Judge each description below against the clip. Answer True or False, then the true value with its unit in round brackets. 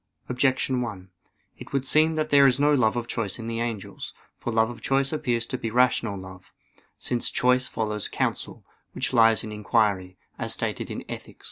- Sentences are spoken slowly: False (190 wpm)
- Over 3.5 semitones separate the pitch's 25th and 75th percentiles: False (3.2 semitones)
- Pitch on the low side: True (120 Hz)